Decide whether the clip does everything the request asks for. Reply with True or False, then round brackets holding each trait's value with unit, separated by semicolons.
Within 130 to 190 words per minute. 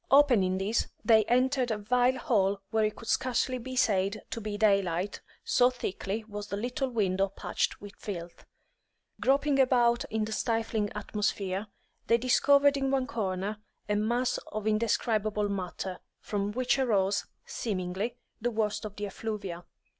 True (150 wpm)